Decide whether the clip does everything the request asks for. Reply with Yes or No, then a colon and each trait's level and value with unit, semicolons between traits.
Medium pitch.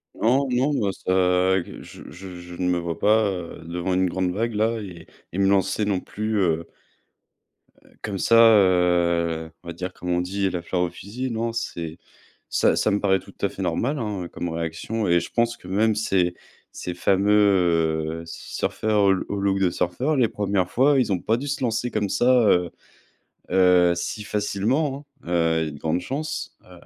No: very low, 95 Hz